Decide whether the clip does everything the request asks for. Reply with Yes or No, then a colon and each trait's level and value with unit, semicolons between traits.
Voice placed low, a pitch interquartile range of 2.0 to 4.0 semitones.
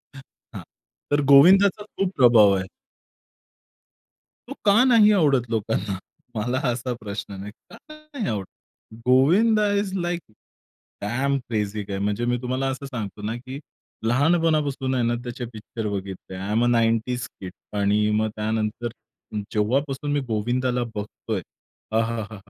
No: low, 120 Hz; average, 4.7 semitones